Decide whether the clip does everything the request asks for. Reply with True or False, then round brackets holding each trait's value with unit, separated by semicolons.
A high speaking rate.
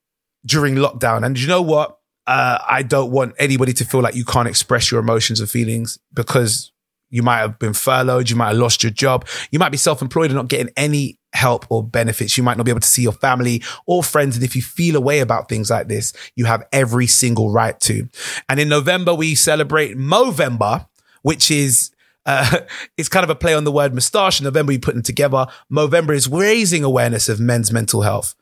True (215 wpm)